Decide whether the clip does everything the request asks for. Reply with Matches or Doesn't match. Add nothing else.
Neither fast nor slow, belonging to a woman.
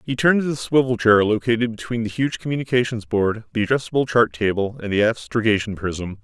Doesn't match